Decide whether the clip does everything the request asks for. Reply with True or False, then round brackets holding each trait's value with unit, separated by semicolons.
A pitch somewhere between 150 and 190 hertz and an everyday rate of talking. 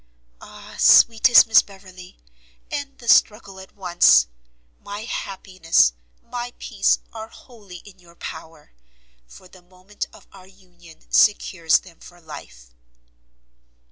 False (185 Hz; 120 wpm)